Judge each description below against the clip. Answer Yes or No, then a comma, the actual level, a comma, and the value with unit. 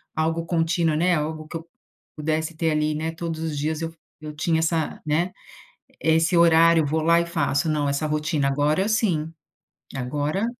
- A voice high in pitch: No, medium, 160 Hz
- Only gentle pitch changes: Yes, narrow, 1.6 semitones